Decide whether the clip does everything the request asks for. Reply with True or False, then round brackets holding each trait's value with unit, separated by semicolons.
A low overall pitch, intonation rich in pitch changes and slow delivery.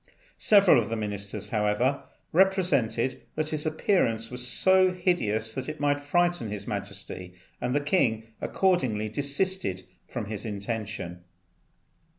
True (120 Hz; 7.0 semitones; 125 wpm)